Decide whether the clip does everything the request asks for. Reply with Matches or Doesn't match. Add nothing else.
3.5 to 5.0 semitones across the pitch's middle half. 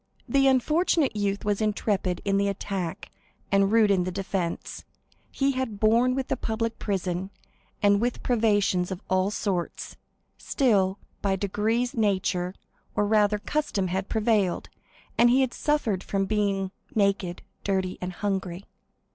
Doesn't match